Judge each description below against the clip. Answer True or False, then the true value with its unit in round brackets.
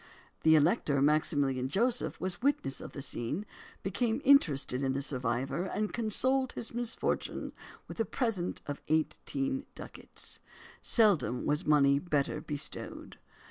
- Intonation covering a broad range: True (8.6 semitones)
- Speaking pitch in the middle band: True (160 Hz)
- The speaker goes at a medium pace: False (130 wpm)